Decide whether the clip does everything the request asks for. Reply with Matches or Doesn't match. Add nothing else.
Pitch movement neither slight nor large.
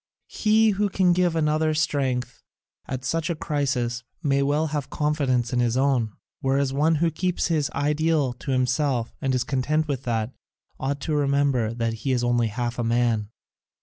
Matches